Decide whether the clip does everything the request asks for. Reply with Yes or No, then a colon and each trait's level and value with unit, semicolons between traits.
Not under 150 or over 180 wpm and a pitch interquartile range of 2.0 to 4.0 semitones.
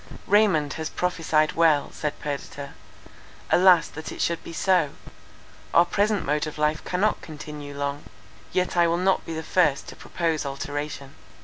Yes: average, 155 wpm; average, 3.3 semitones